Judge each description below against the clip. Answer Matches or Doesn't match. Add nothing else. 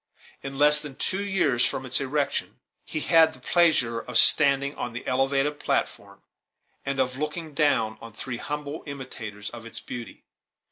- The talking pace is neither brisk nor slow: Matches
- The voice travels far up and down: Doesn't match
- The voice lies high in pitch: Doesn't match